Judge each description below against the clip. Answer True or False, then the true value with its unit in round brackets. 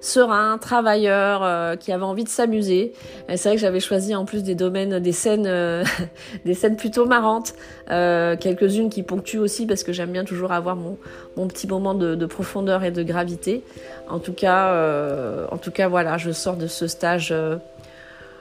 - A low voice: False (185 Hz)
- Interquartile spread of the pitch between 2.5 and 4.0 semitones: True (2.8 semitones)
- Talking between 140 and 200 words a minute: True (195 wpm)